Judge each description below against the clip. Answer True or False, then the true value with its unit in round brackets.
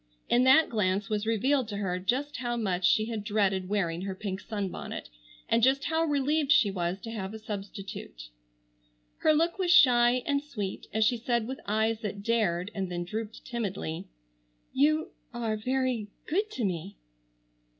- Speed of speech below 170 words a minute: True (160 wpm)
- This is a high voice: True (220 Hz)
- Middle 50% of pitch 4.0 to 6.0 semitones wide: True (4.8 semitones)